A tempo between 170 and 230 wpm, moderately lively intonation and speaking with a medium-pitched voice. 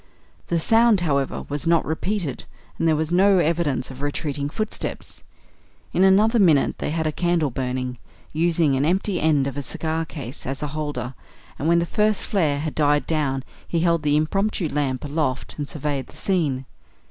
Yes: average, 180 wpm; average, 3.5 semitones; medium, 155 Hz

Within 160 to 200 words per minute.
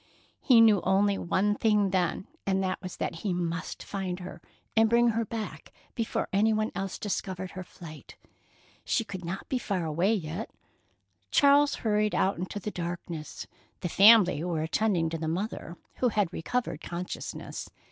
Yes: average, 165 wpm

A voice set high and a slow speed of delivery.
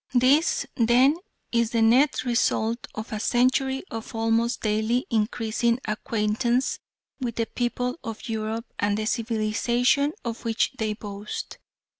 Yes: high, 230 Hz; slow, 130 wpm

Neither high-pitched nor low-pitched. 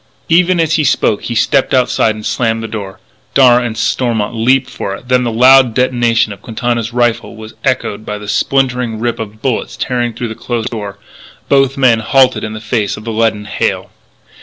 No: low, 120 Hz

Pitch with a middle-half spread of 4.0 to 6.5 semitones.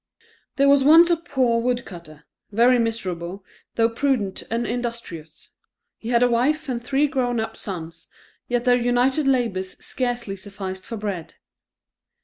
Yes: average, 4.4 semitones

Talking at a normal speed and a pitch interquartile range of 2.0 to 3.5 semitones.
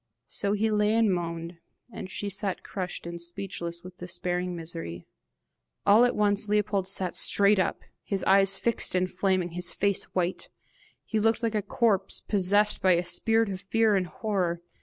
Yes: average, 170 wpm; average, 2.8 semitones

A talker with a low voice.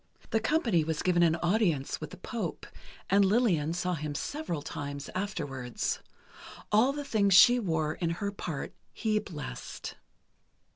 No: medium, 180 Hz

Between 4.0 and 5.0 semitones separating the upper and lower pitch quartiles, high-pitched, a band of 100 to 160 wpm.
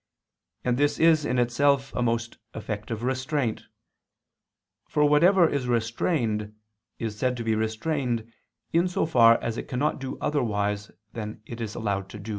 No: average, 4.4 semitones; low, 120 Hz; average, 150 wpm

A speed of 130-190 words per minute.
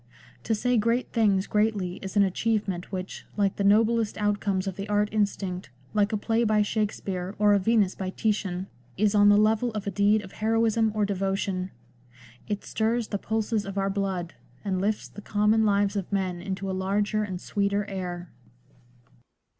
Yes: average, 180 wpm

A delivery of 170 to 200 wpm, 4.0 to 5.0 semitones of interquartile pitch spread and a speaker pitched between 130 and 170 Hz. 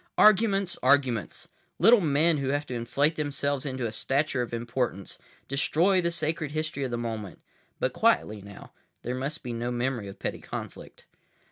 No: average, 160 wpm; average, 4.7 semitones; medium, 140 Hz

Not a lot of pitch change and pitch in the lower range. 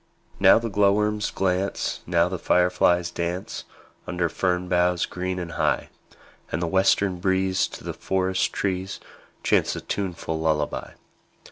Yes: narrow, 1.6 semitones; very low, 90 Hz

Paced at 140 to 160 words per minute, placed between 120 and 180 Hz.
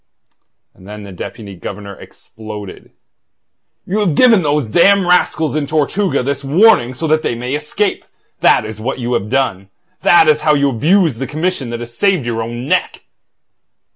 No: average, 170 wpm; medium, 140 Hz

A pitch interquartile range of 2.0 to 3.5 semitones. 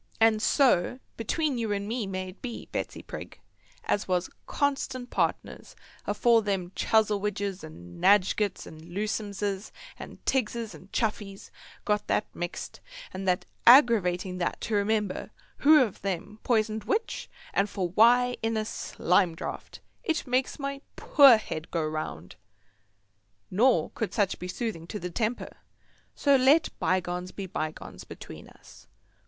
No: average, 4.3 semitones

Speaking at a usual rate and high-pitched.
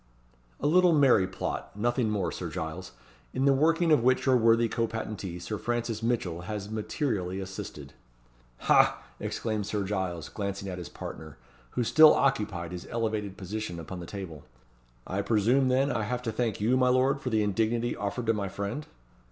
No: average, 175 wpm; low, 110 Hz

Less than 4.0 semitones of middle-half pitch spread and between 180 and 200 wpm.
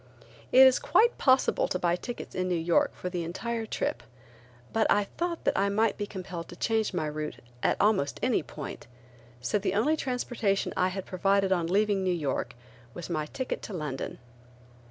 No: average, 4.3 semitones; average, 185 wpm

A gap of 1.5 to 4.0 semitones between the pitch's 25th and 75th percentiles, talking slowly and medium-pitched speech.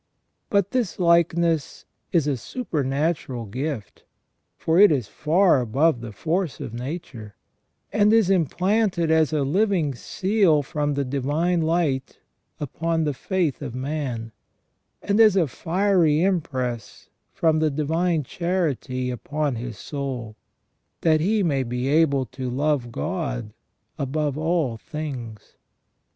No: average, 4.8 semitones; slow, 125 wpm; medium, 150 Hz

